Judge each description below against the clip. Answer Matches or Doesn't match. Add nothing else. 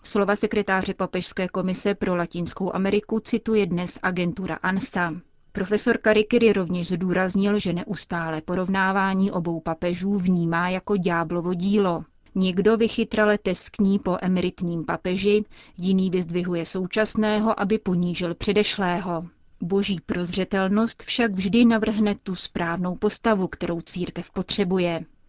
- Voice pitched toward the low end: Doesn't match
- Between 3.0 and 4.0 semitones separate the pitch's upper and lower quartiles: Doesn't match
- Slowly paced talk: Matches